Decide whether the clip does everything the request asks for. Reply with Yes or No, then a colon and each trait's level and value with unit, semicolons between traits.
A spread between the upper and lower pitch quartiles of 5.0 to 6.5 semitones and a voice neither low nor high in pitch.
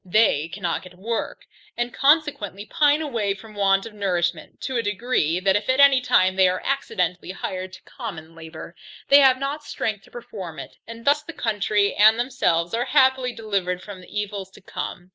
No: wide, 5.5 semitones; high, 210 Hz